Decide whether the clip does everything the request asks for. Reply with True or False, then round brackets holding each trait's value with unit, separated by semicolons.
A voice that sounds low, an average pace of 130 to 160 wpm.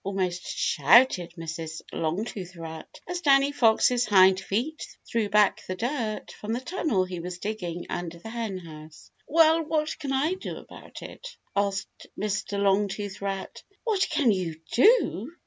False (205 Hz; 145 wpm)